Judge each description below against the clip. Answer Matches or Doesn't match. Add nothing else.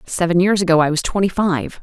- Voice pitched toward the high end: Doesn't match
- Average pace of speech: Doesn't match